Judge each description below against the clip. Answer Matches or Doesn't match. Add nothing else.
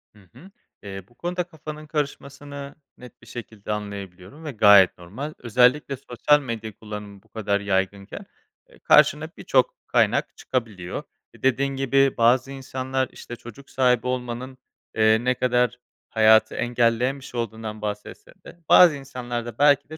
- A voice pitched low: Matches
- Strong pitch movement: Doesn't match